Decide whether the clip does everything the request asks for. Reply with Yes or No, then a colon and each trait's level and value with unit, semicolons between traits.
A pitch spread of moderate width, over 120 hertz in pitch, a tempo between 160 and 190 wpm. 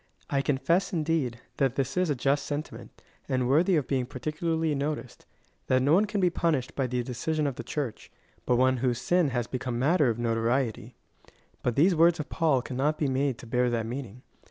No: average, 3.9 semitones; low, 135 Hz; fast, 205 wpm